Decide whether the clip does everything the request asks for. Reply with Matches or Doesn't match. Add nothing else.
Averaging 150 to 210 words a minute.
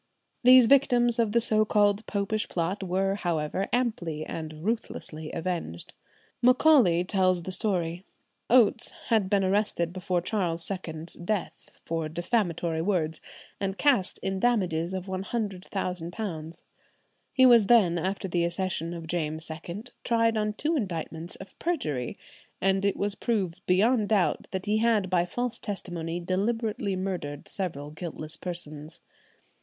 Doesn't match